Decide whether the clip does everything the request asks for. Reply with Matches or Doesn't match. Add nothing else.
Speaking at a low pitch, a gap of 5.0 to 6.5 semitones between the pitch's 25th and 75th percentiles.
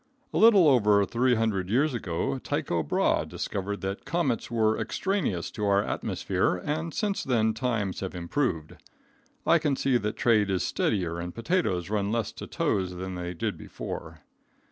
Matches